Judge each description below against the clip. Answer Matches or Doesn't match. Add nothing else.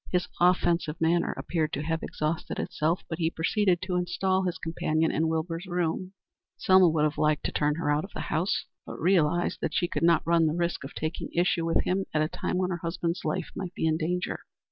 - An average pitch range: Doesn't match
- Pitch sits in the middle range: Matches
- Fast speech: Matches